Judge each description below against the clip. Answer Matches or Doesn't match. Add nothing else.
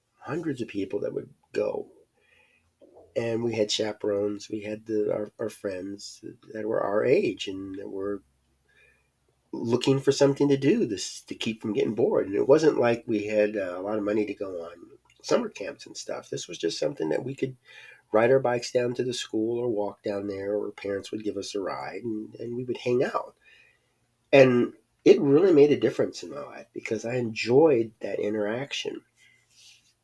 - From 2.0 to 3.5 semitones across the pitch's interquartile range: Matches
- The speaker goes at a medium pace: Matches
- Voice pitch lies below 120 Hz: Matches